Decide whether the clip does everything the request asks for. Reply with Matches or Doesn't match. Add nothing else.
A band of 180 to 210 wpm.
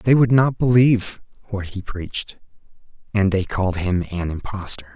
Doesn't match